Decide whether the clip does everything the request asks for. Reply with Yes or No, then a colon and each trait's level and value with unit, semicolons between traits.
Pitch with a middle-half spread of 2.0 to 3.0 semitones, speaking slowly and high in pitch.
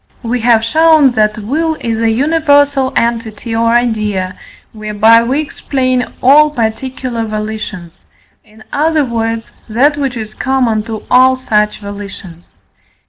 No: average, 3.7 semitones; slow, 130 wpm; high, 230 Hz